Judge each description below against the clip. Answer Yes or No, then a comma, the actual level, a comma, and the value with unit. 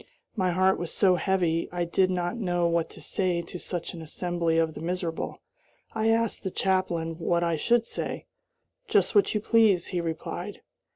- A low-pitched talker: No, medium, 175 Hz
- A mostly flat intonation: Yes, narrow, 2.1 semitones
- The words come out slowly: No, average, 180 wpm